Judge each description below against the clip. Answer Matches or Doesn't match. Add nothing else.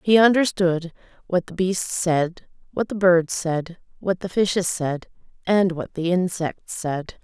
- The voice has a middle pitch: Matches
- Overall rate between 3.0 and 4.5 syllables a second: Matches